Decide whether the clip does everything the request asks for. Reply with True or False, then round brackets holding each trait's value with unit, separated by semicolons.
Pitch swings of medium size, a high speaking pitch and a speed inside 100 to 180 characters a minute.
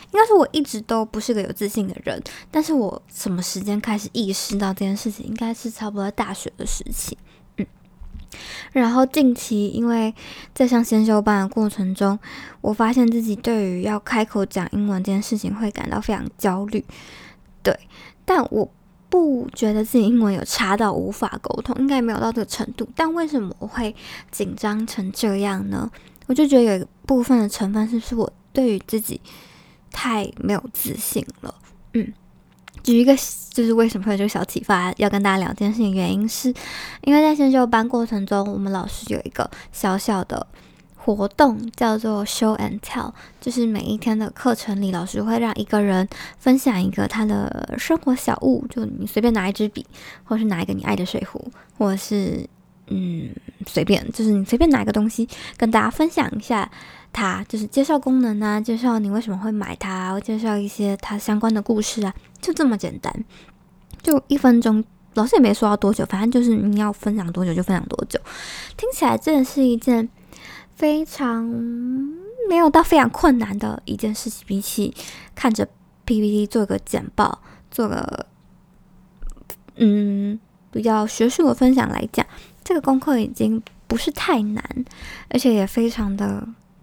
False (3.2 semitones; 220 Hz; 275 characters per minute)